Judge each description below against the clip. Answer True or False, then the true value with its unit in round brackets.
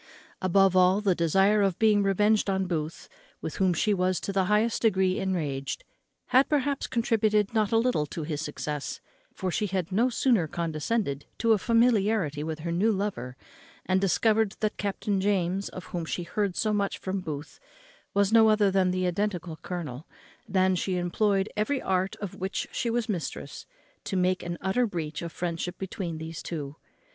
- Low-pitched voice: False (190 Hz)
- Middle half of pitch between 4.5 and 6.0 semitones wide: False (3.6 semitones)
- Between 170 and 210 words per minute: True (180 wpm)